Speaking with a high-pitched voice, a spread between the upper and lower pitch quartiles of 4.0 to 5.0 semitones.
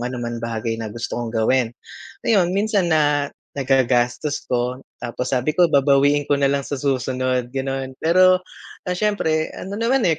No: low, 135 Hz; average, 4.3 semitones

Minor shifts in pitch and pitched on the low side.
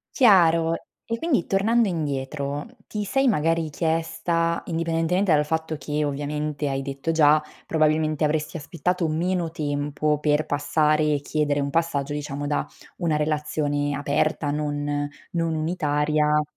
No: narrow, 2.2 semitones; medium, 155 Hz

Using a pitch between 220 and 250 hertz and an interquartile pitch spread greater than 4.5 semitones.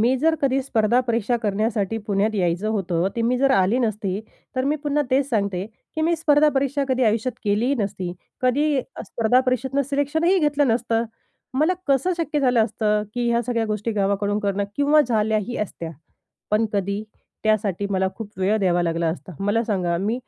Yes: high, 225 Hz; average, 4.9 semitones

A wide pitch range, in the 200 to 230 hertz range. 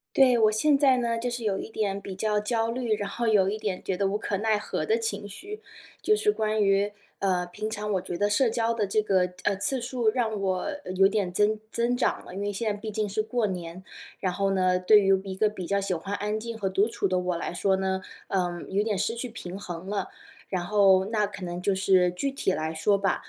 No: average, 2.8 semitones; high, 205 Hz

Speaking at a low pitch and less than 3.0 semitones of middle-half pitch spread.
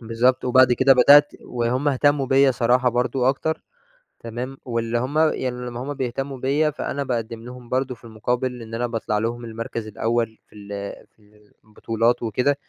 Yes: low, 125 Hz; narrow, 2.4 semitones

